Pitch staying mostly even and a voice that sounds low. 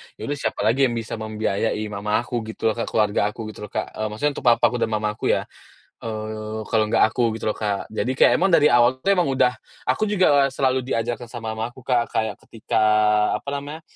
No: average, 3.2 semitones; low, 115 Hz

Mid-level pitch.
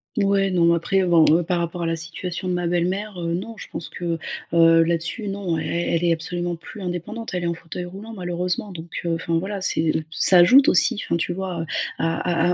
Yes: medium, 175 Hz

